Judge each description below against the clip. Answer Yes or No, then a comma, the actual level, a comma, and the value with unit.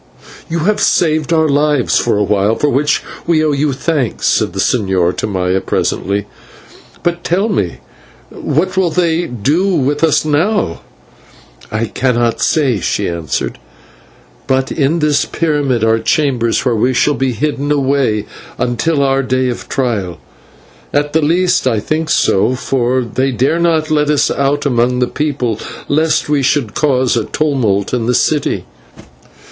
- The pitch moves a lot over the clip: No, average, 4.5 semitones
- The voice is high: No, low, 135 Hz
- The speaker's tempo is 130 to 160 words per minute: Yes, average, 155 wpm